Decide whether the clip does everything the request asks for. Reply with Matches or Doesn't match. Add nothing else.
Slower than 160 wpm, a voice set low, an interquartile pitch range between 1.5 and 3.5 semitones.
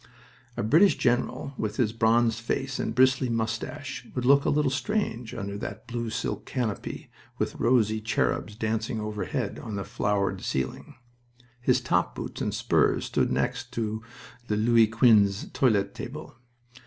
Matches